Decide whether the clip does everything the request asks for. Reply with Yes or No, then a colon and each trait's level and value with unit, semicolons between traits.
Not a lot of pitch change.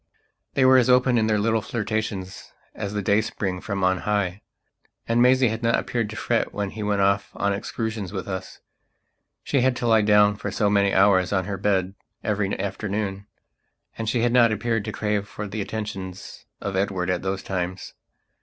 Yes: narrow, 2.3 semitones